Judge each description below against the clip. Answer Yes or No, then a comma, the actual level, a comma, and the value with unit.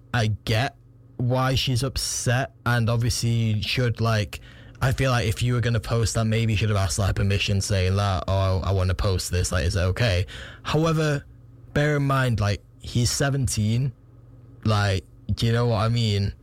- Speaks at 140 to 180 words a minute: No, average, 195 wpm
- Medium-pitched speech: No, low, 115 Hz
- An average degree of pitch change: Yes, average, 3.2 semitones